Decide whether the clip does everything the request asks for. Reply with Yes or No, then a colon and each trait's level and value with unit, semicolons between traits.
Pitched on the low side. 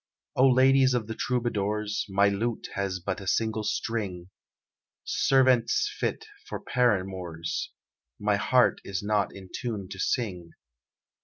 Yes: low, 105 Hz